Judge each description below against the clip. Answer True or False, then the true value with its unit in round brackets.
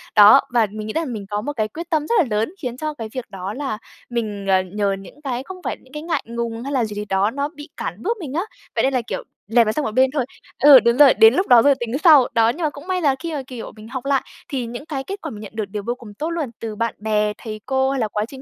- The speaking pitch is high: True (245 Hz)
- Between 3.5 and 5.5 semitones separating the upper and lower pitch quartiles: True (5.1 semitones)